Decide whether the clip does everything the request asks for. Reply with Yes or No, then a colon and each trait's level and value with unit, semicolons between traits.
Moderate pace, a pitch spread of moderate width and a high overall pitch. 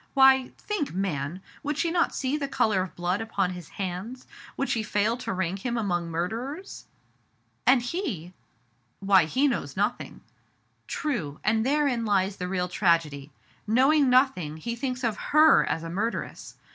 No: average, 170 wpm; wide, 6.7 semitones; high, 210 Hz